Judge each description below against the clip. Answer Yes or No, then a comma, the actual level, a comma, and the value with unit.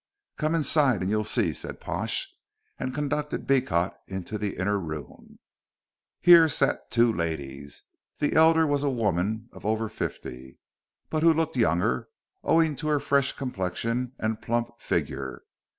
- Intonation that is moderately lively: No, wide, 8.1 semitones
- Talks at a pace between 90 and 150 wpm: Yes, average, 145 wpm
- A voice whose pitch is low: Yes, low, 115 Hz